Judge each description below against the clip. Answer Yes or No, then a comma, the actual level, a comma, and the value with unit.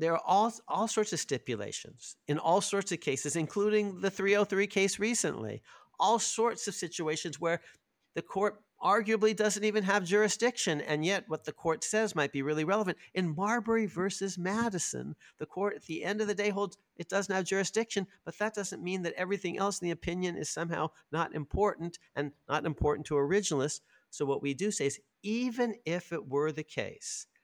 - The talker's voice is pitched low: No, high, 190 Hz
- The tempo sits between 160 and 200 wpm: Yes, average, 190 wpm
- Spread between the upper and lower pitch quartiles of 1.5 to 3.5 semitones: No, average, 4.6 semitones